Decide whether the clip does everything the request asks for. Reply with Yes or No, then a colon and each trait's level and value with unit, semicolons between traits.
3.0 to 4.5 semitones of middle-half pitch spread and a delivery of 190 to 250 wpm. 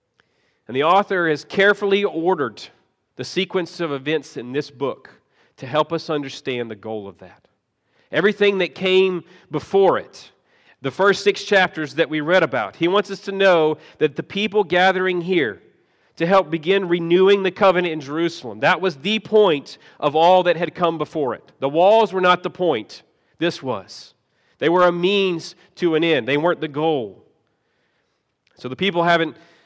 No: average, 3.8 semitones; average, 175 wpm